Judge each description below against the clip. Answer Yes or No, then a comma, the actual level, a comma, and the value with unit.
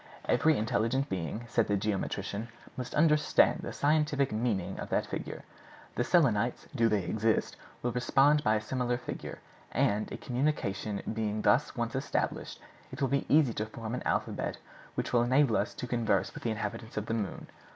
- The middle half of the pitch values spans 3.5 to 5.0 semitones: Yes, average, 3.8 semitones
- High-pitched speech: No, low, 115 Hz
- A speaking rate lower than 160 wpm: No, average, 175 wpm